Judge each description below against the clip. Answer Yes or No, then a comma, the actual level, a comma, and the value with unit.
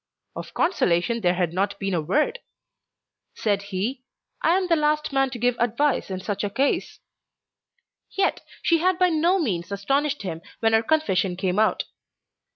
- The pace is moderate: Yes, average, 165 wpm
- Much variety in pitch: Yes, wide, 7.9 semitones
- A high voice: Yes, high, 230 Hz